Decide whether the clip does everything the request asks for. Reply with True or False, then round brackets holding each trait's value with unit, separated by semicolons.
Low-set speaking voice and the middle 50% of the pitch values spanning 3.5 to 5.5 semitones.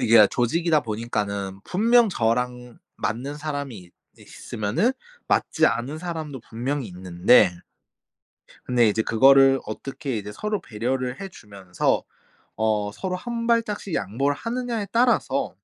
False (125 Hz; 7.6 semitones)